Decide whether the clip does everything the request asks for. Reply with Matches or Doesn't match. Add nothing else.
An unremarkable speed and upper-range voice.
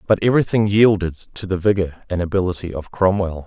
Doesn't match